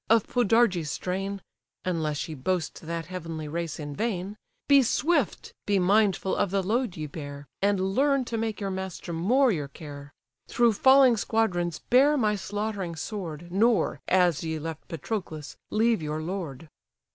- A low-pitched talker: No, high, 190 Hz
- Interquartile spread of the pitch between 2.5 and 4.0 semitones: No, average, 5.3 semitones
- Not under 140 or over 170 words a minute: Yes, average, 155 wpm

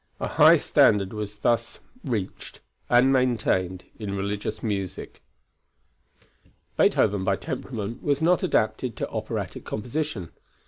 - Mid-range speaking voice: No, low, 110 Hz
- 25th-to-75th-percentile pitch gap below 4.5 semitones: Yes, average, 3.9 semitones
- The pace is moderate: No, slow, 110 wpm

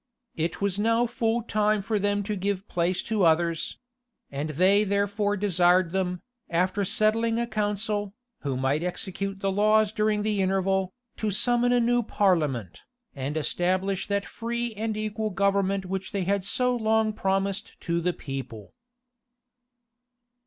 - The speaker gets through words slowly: No, average, 145 wpm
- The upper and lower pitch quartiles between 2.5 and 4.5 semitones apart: Yes, average, 2.9 semitones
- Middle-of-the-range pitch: No, high, 200 Hz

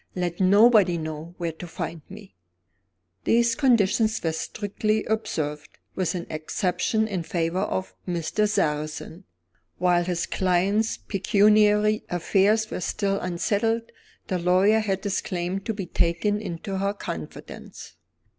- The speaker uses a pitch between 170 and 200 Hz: Yes, high, 190 Hz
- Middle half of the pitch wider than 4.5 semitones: No, average, 3.5 semitones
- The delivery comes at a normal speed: No, slow, 125 wpm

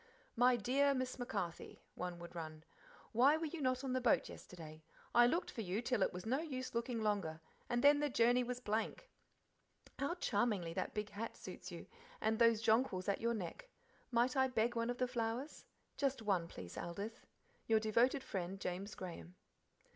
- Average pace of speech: Yes, average, 185 wpm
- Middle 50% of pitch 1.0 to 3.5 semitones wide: No, average, 4.5 semitones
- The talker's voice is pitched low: No, high, 230 Hz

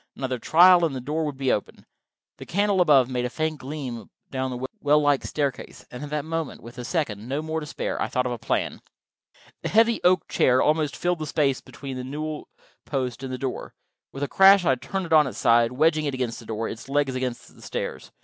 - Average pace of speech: No, fast, 230 wpm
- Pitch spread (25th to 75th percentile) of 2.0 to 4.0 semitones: Yes, average, 3.7 semitones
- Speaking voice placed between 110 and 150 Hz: Yes, medium, 140 Hz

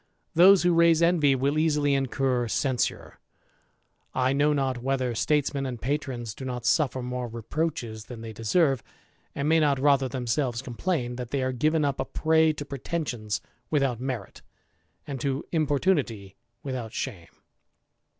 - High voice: No, low, 135 Hz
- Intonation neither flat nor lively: Yes, average, 3.5 semitones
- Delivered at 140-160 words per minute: Yes, average, 150 wpm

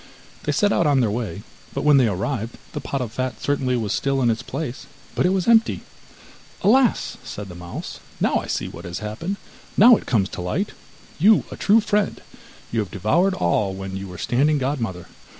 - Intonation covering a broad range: Yes, wide, 8.1 semitones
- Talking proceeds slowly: No, fast, 205 wpm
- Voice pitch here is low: Yes, low, 125 Hz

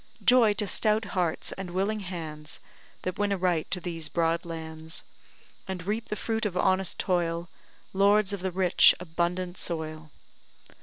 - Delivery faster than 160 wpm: No, average, 155 wpm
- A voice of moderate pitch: Yes, medium, 180 Hz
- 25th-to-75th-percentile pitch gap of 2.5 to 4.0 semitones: Yes, average, 3.0 semitones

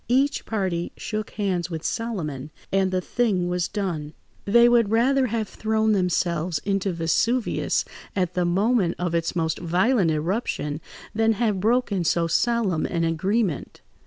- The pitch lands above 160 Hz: Yes, high, 190 Hz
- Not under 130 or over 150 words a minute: Yes, average, 145 wpm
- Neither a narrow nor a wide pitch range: Yes, average, 4.8 semitones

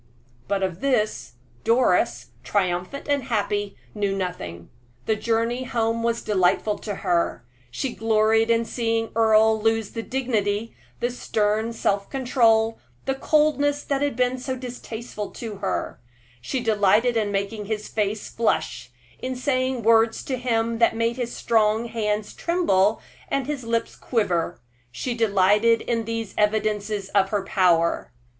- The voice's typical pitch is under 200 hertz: No, high, 225 Hz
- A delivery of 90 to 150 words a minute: Yes, average, 140 wpm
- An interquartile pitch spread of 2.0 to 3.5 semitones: Yes, narrow, 2.6 semitones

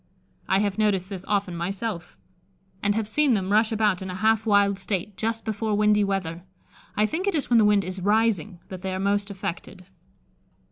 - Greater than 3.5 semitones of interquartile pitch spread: No, narrow, 2.5 semitones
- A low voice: No, high, 205 Hz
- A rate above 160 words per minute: Yes, average, 195 wpm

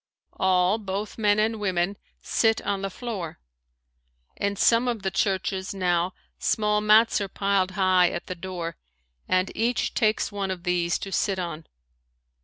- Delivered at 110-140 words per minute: No, average, 155 wpm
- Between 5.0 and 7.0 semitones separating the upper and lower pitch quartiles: No, narrow, 2.4 semitones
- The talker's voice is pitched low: No, high, 195 Hz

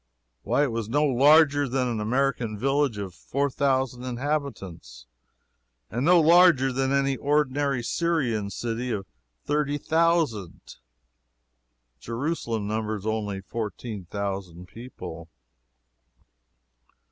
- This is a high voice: No, low, 125 Hz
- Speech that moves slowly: Yes, slow, 105 wpm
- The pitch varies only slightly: No, average, 5.1 semitones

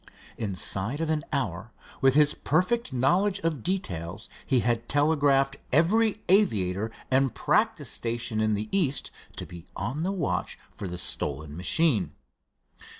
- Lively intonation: Yes, wide, 7.6 semitones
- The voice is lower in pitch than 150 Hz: Yes, low, 135 Hz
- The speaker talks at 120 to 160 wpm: Yes, average, 140 wpm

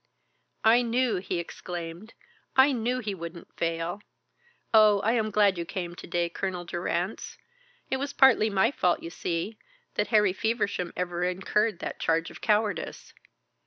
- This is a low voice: No, high, 195 Hz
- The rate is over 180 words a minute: No, average, 155 wpm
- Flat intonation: No, average, 4.3 semitones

